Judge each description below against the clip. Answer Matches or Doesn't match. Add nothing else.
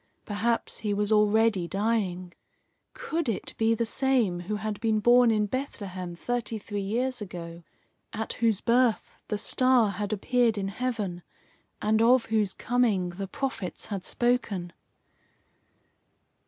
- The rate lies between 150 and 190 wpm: Doesn't match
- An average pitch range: Matches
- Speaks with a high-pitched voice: Matches